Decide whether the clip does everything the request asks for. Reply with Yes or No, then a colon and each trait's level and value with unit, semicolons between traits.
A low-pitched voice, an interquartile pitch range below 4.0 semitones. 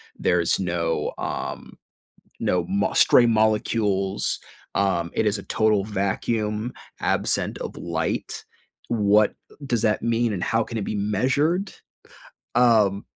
Yes: low, 105 Hz; average, 2.8 semitones